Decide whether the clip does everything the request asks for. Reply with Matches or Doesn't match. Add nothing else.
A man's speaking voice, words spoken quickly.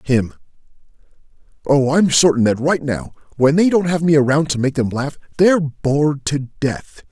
Doesn't match